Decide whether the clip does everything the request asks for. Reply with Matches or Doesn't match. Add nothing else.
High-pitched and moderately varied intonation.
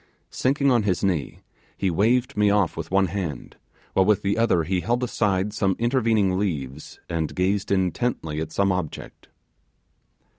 Doesn't match